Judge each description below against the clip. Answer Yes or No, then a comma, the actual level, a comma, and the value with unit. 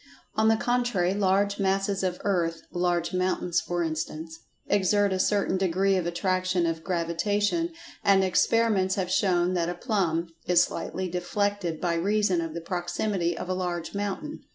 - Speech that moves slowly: No, average, 150 wpm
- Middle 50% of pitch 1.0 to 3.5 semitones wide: Yes, narrow, 2.6 semitones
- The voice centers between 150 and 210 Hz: Yes, medium, 185 Hz